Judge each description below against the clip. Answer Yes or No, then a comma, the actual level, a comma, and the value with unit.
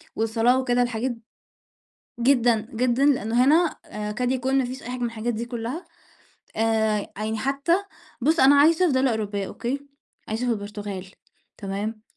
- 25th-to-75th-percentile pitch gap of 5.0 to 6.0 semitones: No, average, 3.3 semitones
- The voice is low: No, high, 240 Hz